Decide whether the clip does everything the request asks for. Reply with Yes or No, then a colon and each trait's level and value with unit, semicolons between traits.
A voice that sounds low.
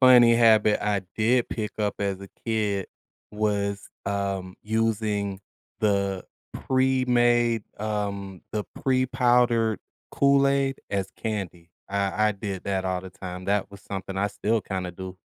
Yes: low, 105 Hz